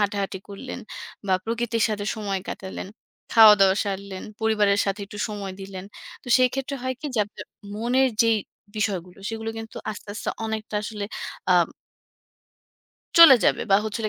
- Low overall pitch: No, high, 215 Hz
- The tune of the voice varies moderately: No, narrow, 2.3 semitones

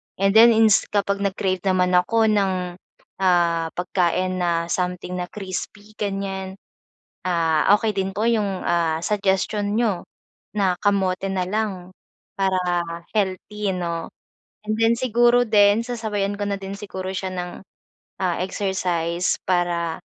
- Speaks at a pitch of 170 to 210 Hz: Yes, high, 190 Hz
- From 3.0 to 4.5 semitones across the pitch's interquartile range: No, narrow, 2.4 semitones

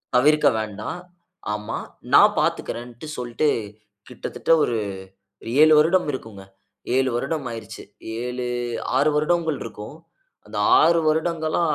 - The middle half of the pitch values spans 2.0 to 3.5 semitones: No, average, 5.0 semitones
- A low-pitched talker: Yes, low, 130 Hz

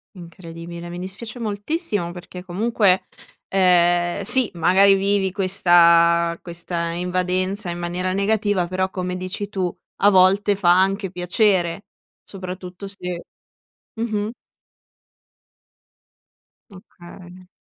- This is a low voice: No, medium, 185 Hz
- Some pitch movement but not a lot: No, narrow, 2.3 semitones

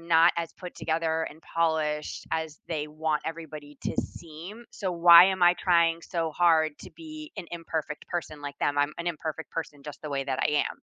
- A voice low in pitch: No, medium, 160 Hz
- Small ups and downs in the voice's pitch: Yes, narrow, 1.8 semitones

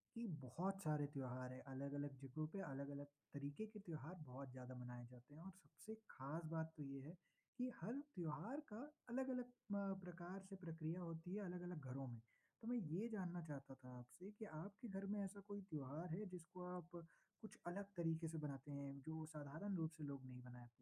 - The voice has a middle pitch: Yes, medium, 160 Hz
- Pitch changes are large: Yes, wide, 5.7 semitones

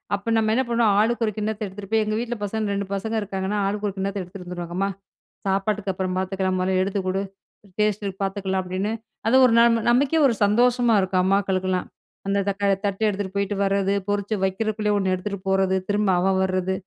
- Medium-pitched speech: No, high, 200 Hz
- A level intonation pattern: Yes, narrow, 2.1 semitones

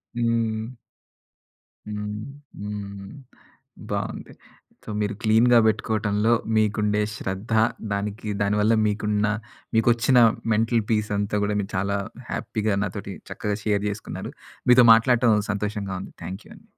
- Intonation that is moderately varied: No, narrow, 1.6 semitones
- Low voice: Yes, low, 105 Hz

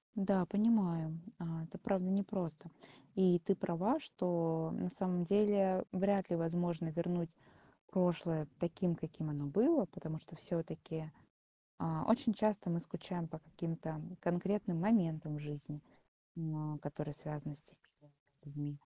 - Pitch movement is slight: No, average, 3.3 semitones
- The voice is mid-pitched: Yes, medium, 170 Hz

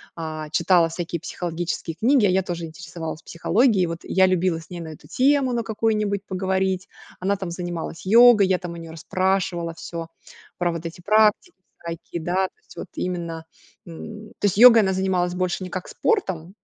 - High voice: No, medium, 180 Hz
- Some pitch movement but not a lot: Yes, average, 3.1 semitones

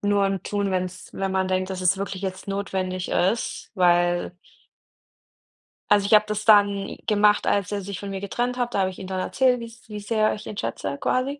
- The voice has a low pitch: No, high, 200 Hz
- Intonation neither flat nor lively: No, narrow, 2.0 semitones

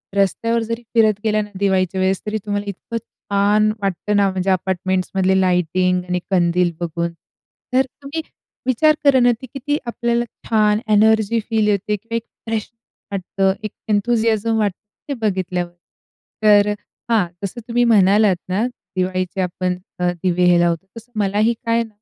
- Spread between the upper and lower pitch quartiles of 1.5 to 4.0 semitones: Yes, average, 3.5 semitones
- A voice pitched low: No, high, 205 Hz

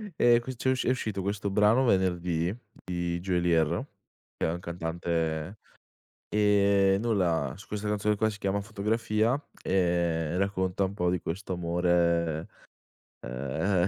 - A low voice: Yes, very low, 95 Hz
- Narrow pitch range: No, average, 3.3 semitones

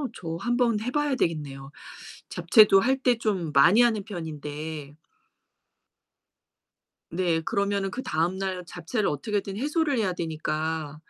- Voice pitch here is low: No, high, 190 Hz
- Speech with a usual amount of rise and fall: No, wide, 6.0 semitones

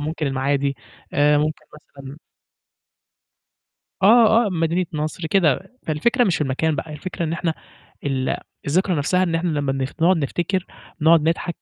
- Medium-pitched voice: Yes, medium, 160 Hz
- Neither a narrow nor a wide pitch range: Yes, average, 3.8 semitones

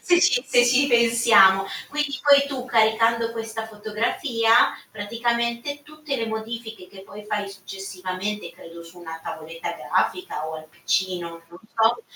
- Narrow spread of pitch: No, average, 3.9 semitones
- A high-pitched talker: Yes, high, 225 Hz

